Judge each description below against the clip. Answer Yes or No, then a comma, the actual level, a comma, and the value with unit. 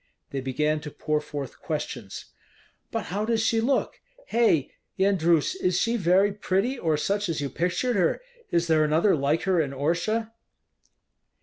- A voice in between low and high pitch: Yes, medium, 170 Hz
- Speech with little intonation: No, average, 5.2 semitones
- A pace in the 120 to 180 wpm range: Yes, average, 160 wpm